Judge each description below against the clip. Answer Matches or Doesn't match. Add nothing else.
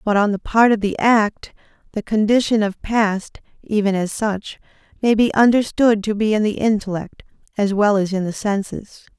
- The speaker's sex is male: Doesn't match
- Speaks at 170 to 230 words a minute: Matches